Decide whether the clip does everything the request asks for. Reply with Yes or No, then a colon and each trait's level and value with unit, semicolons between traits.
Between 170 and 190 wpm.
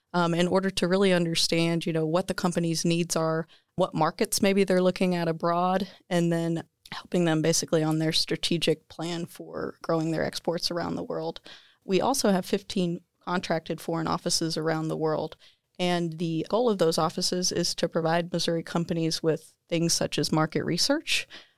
Yes: average, 175 wpm